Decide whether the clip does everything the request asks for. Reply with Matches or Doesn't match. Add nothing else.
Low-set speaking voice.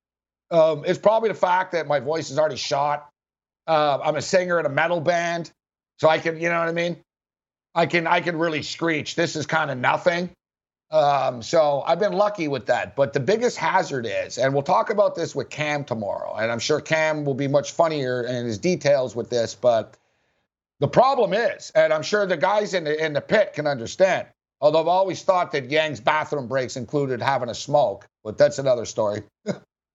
Doesn't match